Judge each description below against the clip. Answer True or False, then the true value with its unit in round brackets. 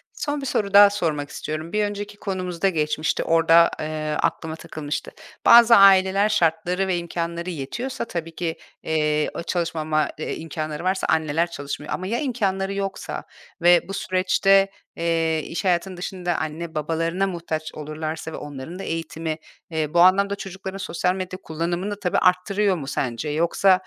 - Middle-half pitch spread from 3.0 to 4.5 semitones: True (3.5 semitones)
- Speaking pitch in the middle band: True (170 Hz)